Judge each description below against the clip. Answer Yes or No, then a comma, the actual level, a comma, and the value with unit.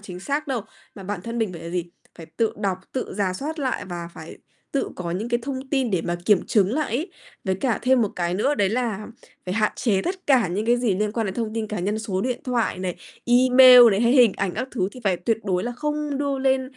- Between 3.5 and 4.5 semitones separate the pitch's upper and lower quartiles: No, average, 5.3 semitones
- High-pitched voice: Yes, high, 225 Hz